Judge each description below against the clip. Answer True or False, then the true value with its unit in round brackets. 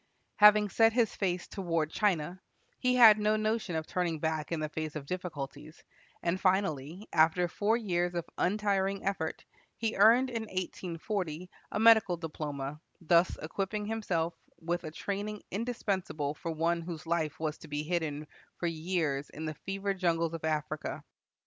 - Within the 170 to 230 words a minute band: False (155 wpm)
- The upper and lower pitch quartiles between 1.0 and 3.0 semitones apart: False (4.3 semitones)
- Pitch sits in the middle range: True (175 Hz)